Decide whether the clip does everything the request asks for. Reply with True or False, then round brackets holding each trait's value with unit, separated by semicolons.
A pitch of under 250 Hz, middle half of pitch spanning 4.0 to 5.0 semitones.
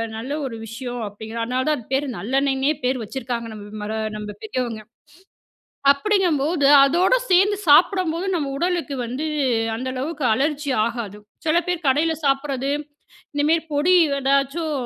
False (275 Hz; 4.7 semitones)